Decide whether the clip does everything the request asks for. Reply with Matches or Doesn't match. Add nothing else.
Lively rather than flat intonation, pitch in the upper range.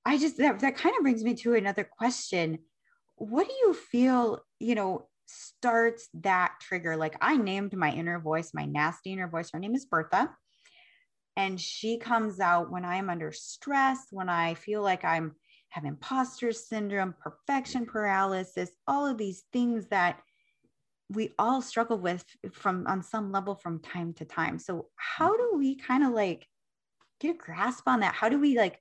Matches